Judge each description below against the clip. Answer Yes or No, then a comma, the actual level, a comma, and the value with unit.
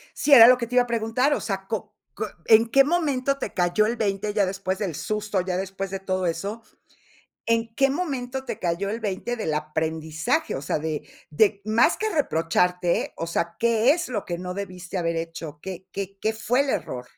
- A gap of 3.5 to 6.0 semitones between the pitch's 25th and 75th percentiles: Yes, average, 4.9 semitones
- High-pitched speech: Yes, high, 200 Hz